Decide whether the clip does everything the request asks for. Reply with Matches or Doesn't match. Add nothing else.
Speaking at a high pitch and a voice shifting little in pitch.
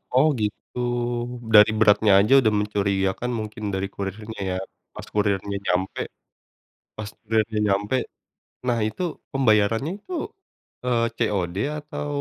Doesn't match